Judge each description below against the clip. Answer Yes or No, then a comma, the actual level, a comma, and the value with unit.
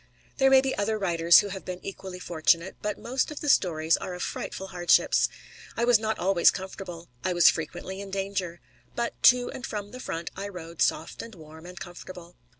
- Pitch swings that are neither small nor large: Yes, average, 3.5 semitones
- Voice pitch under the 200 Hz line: Yes, high, 190 Hz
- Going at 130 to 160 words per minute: No, average, 200 wpm